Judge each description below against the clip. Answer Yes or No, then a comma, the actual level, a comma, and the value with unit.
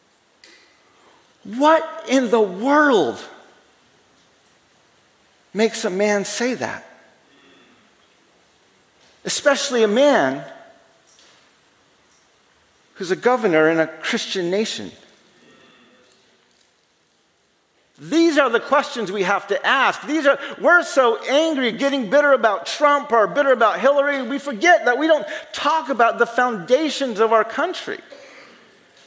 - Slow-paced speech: Yes, slow, 105 wpm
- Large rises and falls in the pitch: No, average, 4.7 semitones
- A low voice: No, very high, 270 Hz